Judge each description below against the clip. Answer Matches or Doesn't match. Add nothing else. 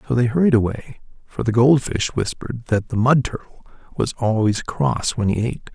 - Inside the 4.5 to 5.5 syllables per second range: Matches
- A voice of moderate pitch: Doesn't match